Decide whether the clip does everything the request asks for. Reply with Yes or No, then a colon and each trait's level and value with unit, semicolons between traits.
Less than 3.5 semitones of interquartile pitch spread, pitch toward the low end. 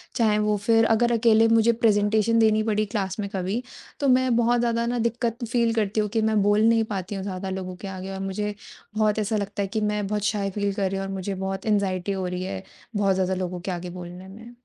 No: average, 2.8 semitones; high, 210 Hz